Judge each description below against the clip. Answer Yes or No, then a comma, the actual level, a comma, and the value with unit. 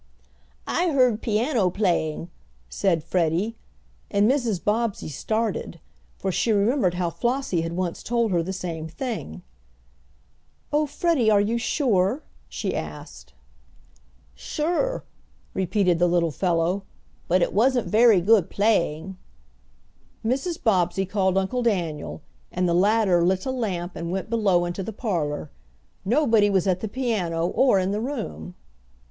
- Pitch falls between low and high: No, high, 195 Hz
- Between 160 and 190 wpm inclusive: No, slow, 135 wpm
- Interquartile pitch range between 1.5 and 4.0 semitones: No, average, 4.9 semitones